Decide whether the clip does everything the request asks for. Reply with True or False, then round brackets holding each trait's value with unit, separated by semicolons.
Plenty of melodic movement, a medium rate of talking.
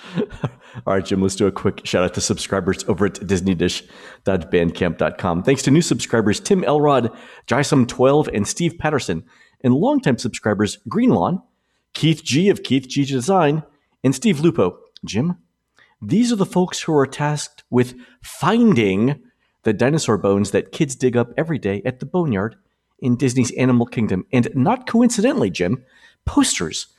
True (7.0 semitones; 150 wpm)